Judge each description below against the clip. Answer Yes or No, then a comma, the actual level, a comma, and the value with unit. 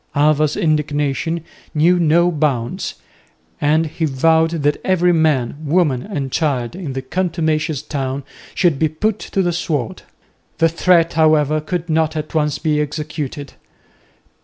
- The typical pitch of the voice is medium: Yes, medium, 155 Hz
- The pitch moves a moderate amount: No, narrow, 2.2 semitones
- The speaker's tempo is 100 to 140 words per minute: Yes, slow, 135 wpm